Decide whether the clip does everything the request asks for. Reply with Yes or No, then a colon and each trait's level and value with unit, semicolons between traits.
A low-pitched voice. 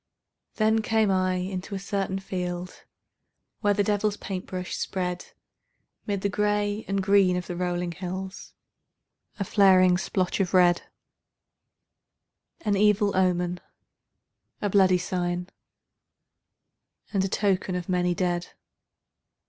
No: high, 190 Hz